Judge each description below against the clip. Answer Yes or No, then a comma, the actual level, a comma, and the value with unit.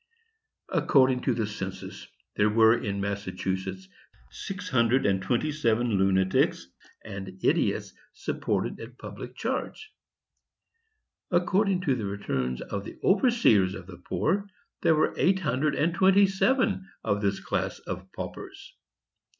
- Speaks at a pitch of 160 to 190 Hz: No, low, 115 Hz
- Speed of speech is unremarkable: No, slow, 130 wpm